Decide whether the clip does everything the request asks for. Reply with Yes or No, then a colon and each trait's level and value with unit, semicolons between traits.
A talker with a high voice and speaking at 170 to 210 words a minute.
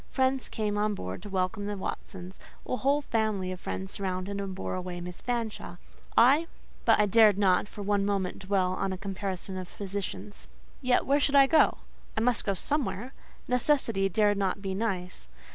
Yes: high, 200 Hz; average, 180 wpm